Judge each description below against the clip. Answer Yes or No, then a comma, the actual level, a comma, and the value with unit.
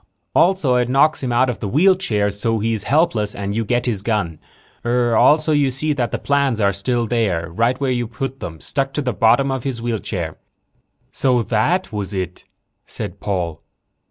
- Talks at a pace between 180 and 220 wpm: Yes, average, 185 wpm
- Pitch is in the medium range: No, low, 120 Hz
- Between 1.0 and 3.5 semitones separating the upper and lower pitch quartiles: No, average, 4.7 semitones